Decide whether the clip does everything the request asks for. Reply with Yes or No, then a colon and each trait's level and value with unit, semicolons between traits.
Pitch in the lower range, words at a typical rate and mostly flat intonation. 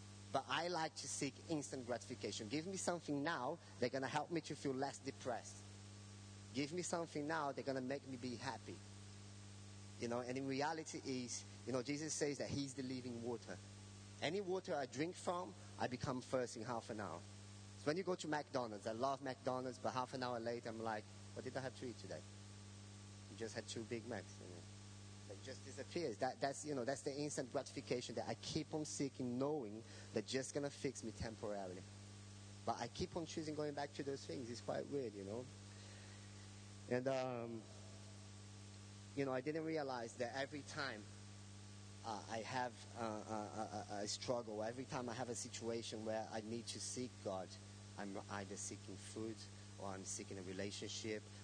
No: low, 115 Hz; average, 190 wpm; average, 4.7 semitones